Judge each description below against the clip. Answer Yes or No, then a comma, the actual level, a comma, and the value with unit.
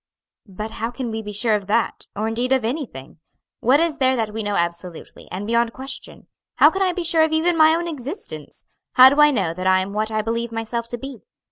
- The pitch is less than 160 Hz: No, high, 230 Hz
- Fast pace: Yes, fast, 235 wpm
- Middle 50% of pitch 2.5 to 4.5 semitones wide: No, average, 4.9 semitones